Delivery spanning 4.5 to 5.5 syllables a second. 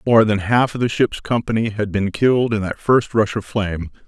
Yes: 5.1 syllables/s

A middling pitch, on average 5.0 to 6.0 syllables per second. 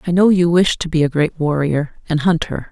Yes: medium, 165 Hz; 5.2 syllables/s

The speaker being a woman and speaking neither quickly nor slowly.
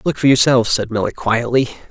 No: male; average, 190 wpm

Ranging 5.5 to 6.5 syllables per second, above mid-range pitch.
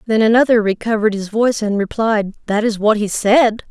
Yes: 5.6 syllables/s; high, 215 Hz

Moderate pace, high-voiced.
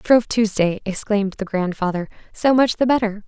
Yes: average, 165 wpm; high, 210 Hz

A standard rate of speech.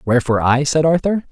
Yes: average, 180 wpm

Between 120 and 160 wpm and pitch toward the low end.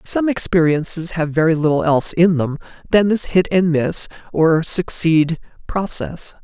No: average, 150 wpm; medium, 170 Hz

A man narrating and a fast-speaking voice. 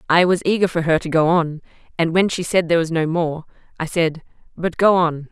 No: female; fast, 235 wpm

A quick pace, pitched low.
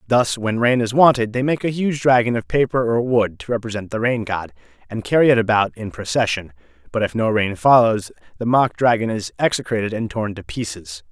Yes: fast, 210 wpm; low, 110 Hz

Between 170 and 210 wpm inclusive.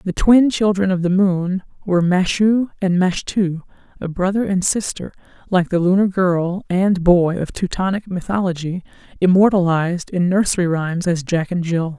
No: average, 155 wpm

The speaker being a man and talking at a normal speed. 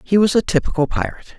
No: male; fast, 215 wpm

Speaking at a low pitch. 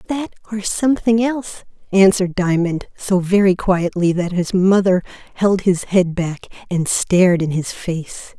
No: high, 190 Hz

